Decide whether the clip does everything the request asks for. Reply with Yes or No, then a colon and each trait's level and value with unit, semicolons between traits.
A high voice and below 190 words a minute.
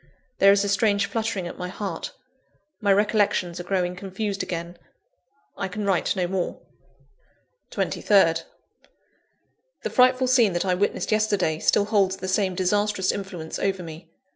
Yes: high, 195 Hz; average, 145 wpm